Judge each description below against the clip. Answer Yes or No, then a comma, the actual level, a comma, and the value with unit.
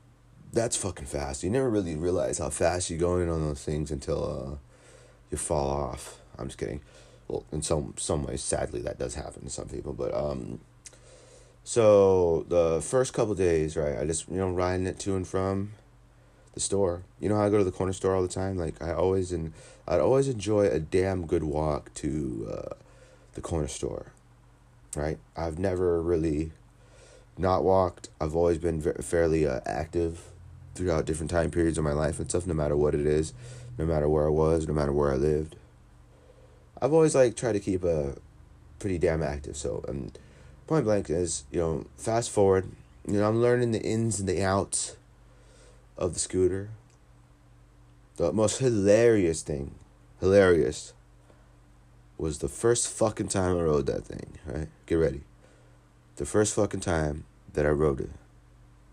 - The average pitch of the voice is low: Yes, very low, 85 Hz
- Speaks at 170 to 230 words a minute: Yes, average, 180 wpm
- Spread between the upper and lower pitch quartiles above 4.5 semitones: Yes, average, 5.2 semitones